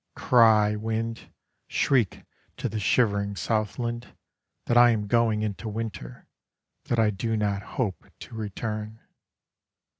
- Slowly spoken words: Yes, slow, 120 wpm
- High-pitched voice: No, low, 110 Hz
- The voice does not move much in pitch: Yes, narrow, 1.8 semitones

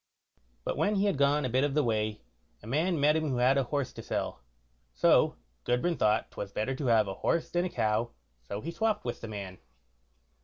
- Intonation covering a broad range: Yes, wide, 6.0 semitones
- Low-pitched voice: Yes, low, 130 Hz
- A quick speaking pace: Yes, fast, 220 wpm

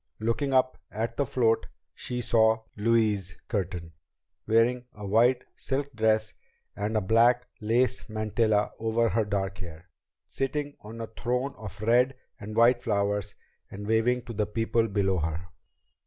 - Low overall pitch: Yes, low, 110 Hz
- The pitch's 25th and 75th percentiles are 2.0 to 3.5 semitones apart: Yes, average, 2.7 semitones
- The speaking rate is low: No, average, 145 wpm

